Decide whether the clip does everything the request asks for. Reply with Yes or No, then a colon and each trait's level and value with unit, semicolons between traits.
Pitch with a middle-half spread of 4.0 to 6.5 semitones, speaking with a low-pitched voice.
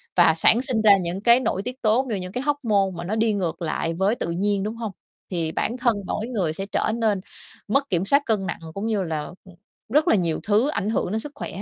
No: average, 4.3 semitones; high, 210 Hz